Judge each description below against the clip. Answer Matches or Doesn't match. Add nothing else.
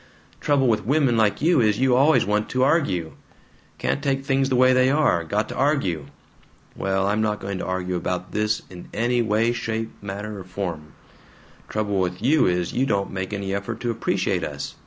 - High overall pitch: Doesn't match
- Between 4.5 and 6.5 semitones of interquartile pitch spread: Matches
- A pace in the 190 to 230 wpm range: Matches